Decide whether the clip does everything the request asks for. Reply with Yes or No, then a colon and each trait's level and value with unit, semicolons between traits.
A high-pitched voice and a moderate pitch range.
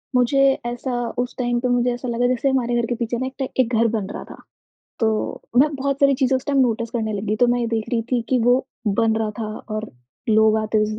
No: high, 240 Hz; narrow, 2.2 semitones